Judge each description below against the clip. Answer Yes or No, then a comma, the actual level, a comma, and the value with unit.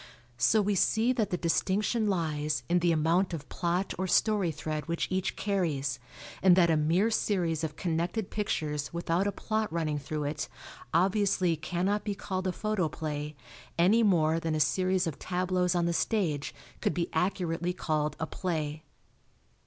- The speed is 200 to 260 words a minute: No, average, 165 wpm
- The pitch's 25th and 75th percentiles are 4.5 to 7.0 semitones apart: No, average, 3.4 semitones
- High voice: No, medium, 175 Hz